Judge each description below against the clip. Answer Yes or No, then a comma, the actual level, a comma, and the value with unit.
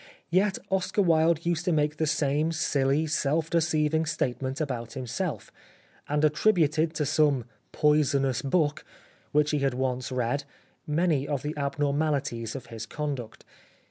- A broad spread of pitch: No, average, 2.7 semitones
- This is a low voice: No, medium, 150 Hz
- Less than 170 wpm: Yes, average, 150 wpm